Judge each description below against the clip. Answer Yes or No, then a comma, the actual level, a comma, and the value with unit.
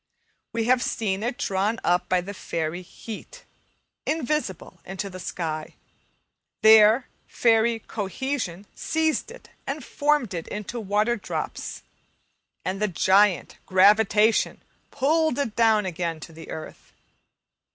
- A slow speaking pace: Yes, slow, 120 wpm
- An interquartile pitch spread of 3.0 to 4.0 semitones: No, average, 4.4 semitones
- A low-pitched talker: No, high, 210 Hz